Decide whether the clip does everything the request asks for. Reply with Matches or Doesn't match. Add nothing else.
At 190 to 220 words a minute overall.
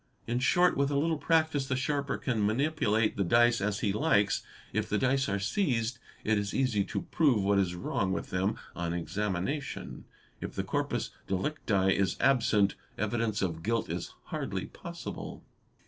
Doesn't match